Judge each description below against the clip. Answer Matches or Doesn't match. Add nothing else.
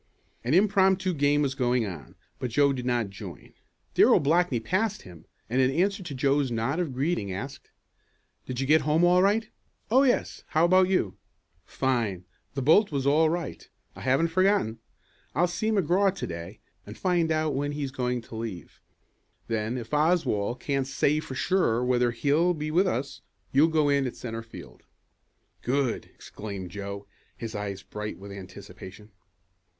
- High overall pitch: Doesn't match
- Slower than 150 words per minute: Doesn't match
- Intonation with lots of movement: Matches